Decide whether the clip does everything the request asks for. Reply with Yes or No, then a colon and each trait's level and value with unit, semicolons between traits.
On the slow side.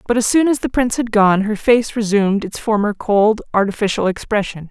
No: fast, 205 wpm